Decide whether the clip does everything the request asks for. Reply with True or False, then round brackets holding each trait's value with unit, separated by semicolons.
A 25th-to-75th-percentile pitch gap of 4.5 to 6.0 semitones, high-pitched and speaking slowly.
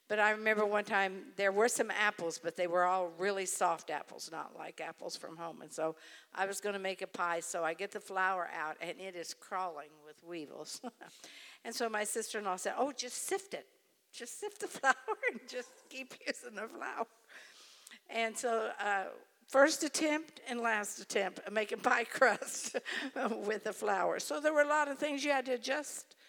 False (5.6 semitones; 215 Hz; 205 wpm)